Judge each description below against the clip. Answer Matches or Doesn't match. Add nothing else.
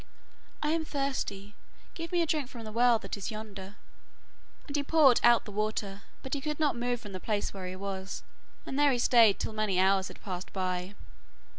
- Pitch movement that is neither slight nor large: Doesn't match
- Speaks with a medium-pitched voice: Doesn't match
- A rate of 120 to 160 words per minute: Doesn't match